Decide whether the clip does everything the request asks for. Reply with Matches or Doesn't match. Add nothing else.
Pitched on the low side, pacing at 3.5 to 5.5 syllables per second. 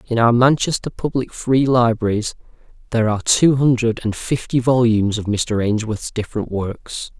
Matches